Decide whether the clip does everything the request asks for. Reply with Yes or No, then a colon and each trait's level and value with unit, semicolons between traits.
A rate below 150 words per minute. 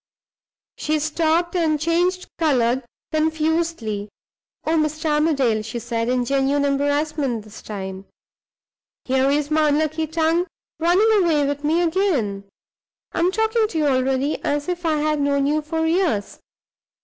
Yes: average, 140 wpm